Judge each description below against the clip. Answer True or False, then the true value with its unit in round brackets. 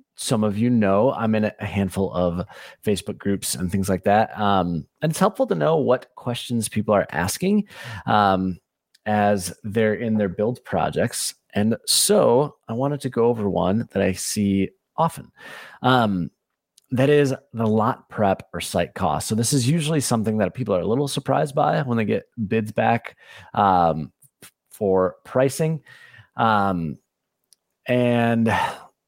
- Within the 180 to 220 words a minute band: False (155 wpm)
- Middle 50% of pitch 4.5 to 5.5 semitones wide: True (4.8 semitones)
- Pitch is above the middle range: False (110 Hz)